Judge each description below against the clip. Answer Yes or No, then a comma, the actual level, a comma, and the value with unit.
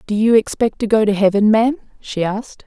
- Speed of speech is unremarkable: No, fast, 225 wpm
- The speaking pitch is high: Yes, high, 215 Hz